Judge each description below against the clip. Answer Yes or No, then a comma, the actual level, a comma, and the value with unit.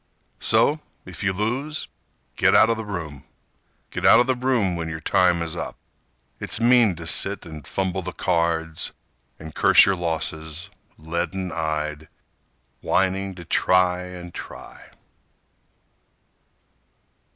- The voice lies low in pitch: Yes, very low, 90 Hz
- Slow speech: Yes, slow, 130 wpm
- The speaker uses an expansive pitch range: No, average, 3.2 semitones